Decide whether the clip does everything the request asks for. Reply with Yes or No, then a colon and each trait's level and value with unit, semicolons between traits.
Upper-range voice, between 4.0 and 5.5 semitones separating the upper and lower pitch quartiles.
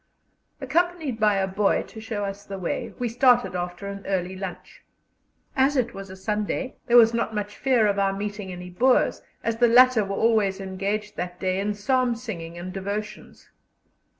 No: high, 205 Hz; average, 3.4 semitones